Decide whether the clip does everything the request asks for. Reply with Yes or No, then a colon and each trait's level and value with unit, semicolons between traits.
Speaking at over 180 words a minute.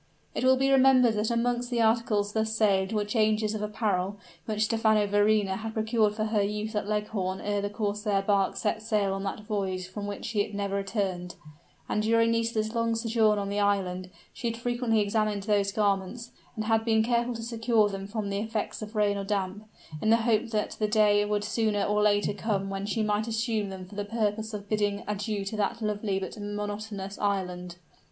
Yes: average, 200 wpm